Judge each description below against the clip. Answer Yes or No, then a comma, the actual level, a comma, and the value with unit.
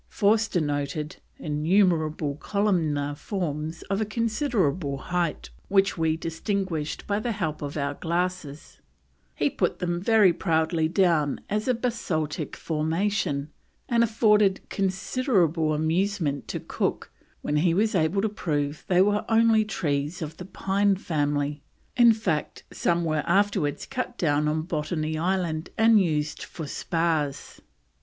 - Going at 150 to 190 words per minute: No, slow, 135 wpm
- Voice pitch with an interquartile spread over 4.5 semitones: Yes, average, 4.9 semitones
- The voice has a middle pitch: Yes, medium, 170 Hz